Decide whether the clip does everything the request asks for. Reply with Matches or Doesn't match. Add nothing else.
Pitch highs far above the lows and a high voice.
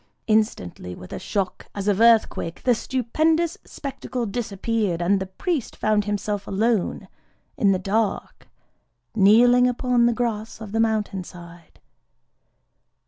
Doesn't match